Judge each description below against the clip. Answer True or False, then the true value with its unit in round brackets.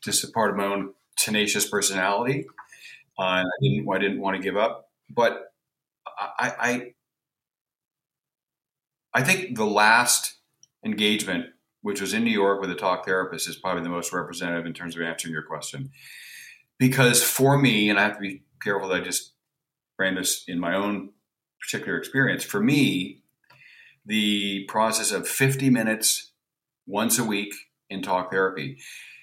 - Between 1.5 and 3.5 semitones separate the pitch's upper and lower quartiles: False (4.7 semitones)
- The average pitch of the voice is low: True (100 Hz)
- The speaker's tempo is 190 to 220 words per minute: False (155 wpm)